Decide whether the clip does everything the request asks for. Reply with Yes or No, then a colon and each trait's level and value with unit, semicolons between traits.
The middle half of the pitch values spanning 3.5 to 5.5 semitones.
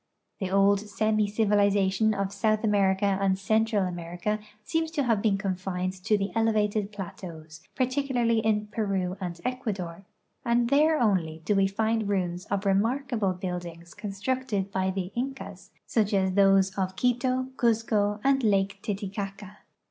No: average, 2.7 semitones